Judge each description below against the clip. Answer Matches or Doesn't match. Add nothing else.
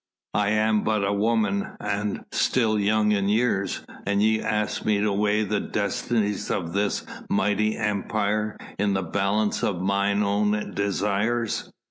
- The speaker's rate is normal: Matches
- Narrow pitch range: Matches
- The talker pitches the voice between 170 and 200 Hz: Doesn't match